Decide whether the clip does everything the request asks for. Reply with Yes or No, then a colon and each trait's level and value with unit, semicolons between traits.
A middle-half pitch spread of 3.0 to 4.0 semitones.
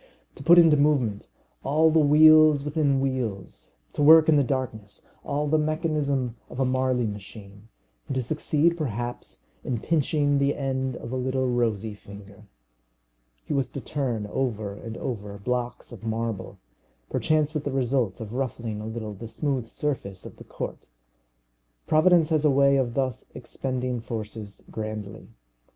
No: average, 4.7 semitones